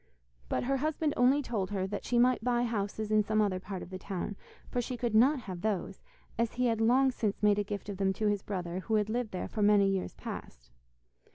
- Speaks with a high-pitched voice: Yes, high, 210 Hz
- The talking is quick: Yes, fast, 240 wpm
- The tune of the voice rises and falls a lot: No, average, 3.6 semitones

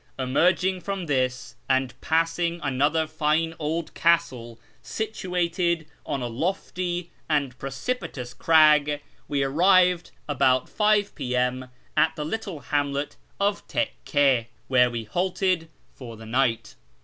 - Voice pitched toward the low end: No, medium, 155 Hz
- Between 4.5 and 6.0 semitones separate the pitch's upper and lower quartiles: Yes, average, 5.2 semitones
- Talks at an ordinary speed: No, slow, 115 wpm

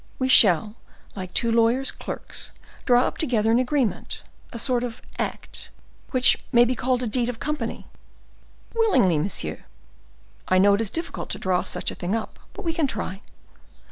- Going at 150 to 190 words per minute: Yes, average, 170 wpm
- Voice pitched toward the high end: Yes, high, 235 Hz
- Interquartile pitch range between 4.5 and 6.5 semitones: No, average, 3.9 semitones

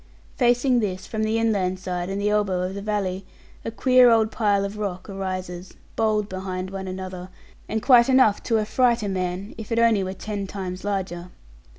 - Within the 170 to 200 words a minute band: Yes, average, 190 wpm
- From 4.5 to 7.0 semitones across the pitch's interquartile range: No, average, 2.9 semitones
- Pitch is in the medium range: No, high, 200 Hz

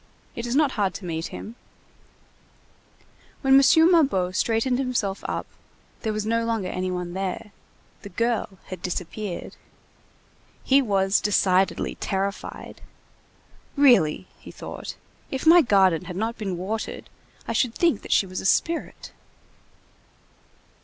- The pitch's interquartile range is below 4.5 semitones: No, average, 4.9 semitones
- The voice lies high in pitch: Yes, high, 210 Hz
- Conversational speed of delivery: No, slow, 130 wpm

